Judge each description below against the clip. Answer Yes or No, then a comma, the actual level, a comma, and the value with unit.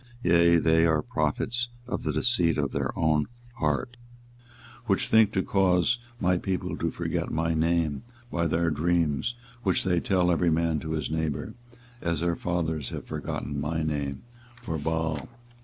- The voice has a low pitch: Yes, very low, 85 Hz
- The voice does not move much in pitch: Yes, narrow, 2.2 semitones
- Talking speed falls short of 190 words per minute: Yes, average, 160 wpm